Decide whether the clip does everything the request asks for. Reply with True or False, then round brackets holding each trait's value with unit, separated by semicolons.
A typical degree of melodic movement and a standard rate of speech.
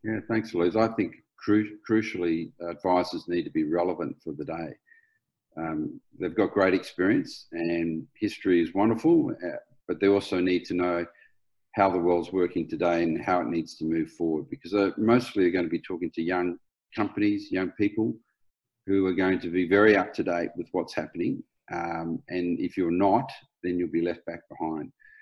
True (4.3 semitones; 185 wpm)